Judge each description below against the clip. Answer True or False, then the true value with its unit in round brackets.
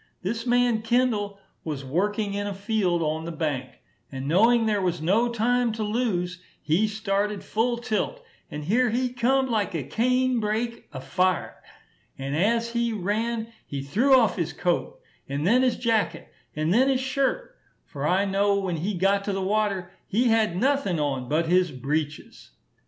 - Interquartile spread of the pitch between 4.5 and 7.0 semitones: True (5.5 semitones)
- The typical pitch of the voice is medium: False (205 Hz)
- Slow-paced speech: False (170 wpm)